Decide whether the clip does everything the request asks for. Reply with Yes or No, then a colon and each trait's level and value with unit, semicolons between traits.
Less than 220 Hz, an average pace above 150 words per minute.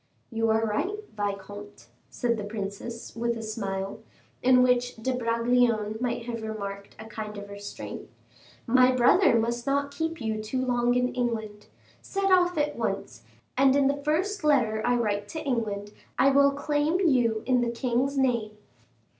No: high, 235 Hz; average, 165 wpm